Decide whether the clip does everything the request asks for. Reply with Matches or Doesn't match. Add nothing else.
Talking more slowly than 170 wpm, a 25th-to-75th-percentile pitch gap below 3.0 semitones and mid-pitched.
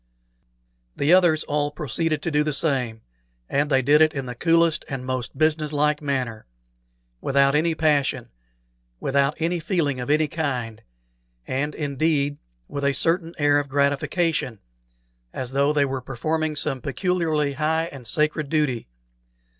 Matches